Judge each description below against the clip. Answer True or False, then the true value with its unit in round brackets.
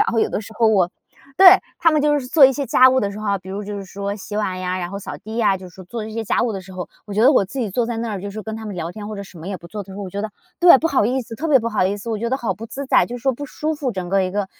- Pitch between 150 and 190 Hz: False (215 Hz)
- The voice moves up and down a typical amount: True (4.0 semitones)